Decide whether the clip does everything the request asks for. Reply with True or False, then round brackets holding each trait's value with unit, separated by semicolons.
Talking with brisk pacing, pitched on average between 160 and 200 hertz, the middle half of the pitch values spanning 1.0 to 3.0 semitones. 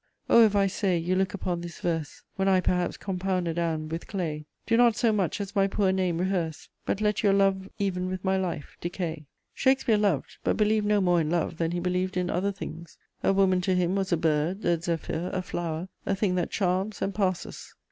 True (220 wpm; 185 Hz; 2.4 semitones)